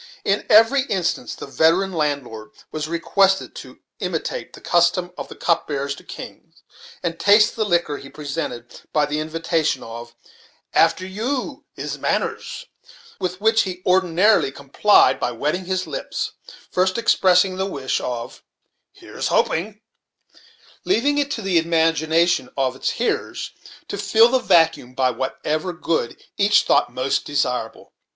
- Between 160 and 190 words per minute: No, average, 145 wpm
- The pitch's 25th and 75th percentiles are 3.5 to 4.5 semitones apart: No, average, 5.3 semitones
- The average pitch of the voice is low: No, medium, 170 Hz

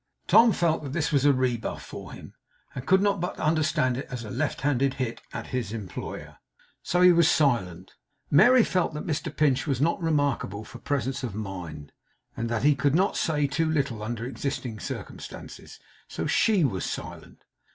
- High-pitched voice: No, medium, 140 Hz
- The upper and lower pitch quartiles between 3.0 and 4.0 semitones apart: No, average, 5.3 semitones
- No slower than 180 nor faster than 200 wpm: Yes, average, 185 wpm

